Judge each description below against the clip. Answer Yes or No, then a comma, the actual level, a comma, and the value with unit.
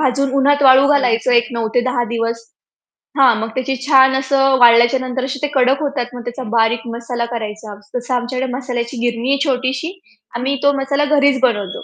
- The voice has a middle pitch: No, very high, 255 Hz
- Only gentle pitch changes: Yes, narrow, 2.3 semitones